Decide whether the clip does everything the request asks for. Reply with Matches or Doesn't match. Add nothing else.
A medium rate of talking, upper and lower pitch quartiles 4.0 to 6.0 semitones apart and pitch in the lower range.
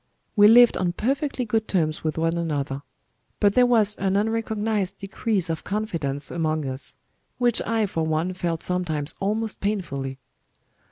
Doesn't match